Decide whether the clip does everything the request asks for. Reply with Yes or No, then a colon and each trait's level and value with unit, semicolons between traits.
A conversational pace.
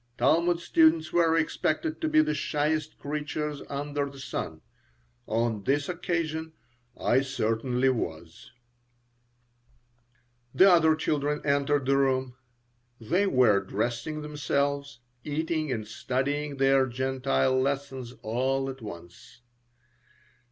No: slow, 110 wpm